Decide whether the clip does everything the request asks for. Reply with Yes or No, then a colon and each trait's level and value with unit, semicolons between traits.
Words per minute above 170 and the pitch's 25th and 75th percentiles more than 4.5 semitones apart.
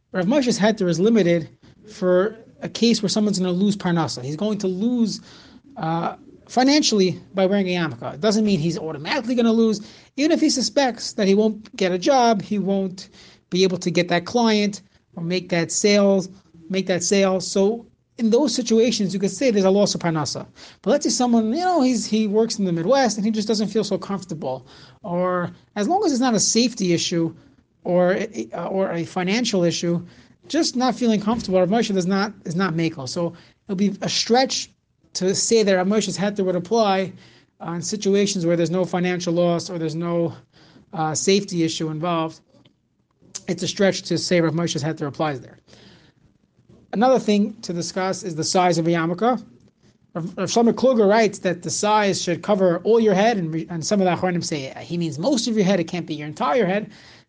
No: average, 200 wpm; average, 4.1 semitones